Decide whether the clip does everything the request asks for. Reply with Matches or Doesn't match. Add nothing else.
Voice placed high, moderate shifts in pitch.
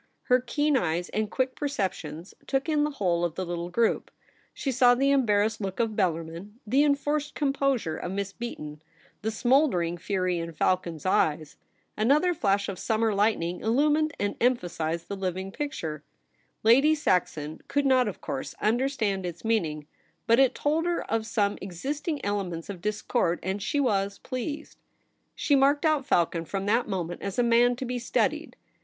Doesn't match